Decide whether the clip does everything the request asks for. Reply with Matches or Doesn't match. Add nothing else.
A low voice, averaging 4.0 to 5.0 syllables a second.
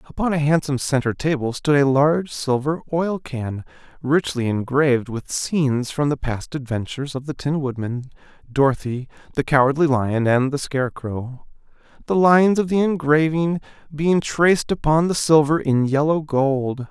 Doesn't match